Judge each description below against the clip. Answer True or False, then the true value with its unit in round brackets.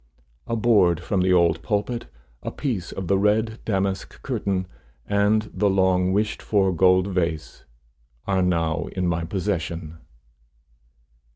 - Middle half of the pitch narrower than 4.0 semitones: True (2.9 semitones)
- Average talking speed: False (130 wpm)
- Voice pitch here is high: False (95 Hz)